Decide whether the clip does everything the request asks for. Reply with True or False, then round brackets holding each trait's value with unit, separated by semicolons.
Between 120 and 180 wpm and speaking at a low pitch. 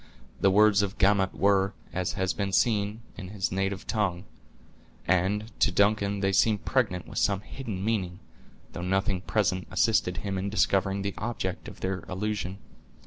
True (160 wpm; 100 Hz)